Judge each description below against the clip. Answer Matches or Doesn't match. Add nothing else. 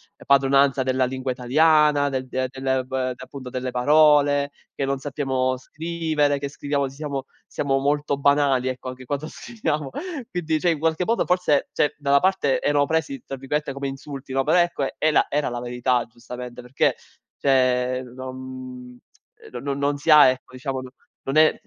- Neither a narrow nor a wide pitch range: Doesn't match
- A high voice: Doesn't match